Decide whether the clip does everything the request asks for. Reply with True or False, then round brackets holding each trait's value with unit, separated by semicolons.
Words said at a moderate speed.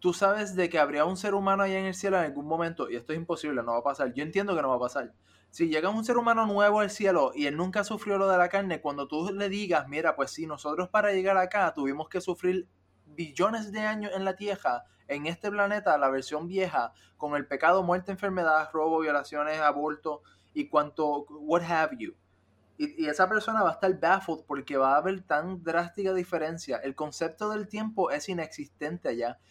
False (220 wpm)